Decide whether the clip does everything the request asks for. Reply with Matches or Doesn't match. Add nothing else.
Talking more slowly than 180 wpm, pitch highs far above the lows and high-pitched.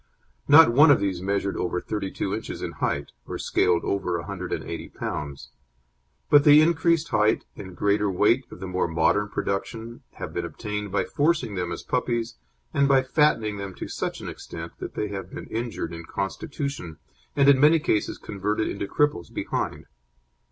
Doesn't match